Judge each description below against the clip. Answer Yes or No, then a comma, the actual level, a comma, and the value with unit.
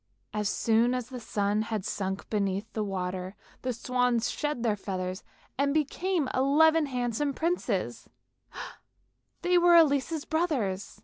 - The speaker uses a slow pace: Yes, slow, 130 wpm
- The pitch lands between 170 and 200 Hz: No, high, 245 Hz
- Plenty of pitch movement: Yes, wide, 6.4 semitones